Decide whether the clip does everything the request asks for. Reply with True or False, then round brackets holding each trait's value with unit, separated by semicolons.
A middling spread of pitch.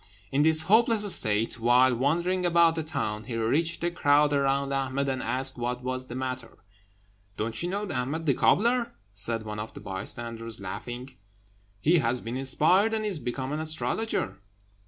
False (5.7 semitones)